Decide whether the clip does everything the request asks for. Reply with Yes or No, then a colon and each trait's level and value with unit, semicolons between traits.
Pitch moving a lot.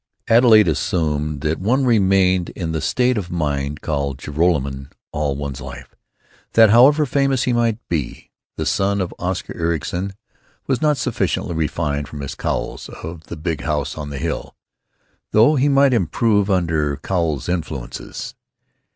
Yes: wide, 6.9 semitones